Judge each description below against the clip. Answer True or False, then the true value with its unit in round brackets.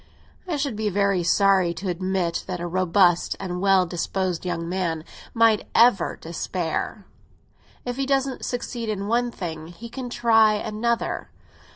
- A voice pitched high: True (195 Hz)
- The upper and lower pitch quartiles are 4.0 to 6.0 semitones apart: True (4.7 semitones)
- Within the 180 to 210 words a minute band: False (150 wpm)